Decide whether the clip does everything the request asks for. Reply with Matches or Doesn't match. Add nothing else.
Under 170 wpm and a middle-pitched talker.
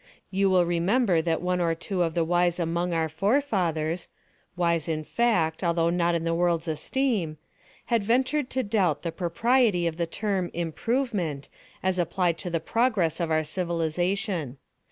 Matches